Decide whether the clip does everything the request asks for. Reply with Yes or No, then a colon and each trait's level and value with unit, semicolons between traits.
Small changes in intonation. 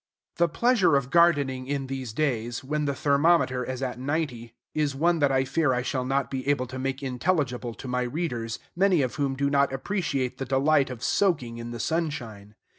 No: average, 3.3 semitones